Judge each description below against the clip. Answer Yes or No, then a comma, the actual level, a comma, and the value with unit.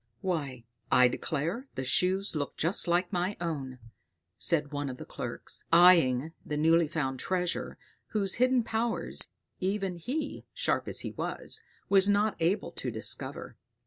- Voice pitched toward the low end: No, medium, 170 Hz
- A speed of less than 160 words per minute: Yes, average, 145 wpm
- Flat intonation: No, average, 4.9 semitones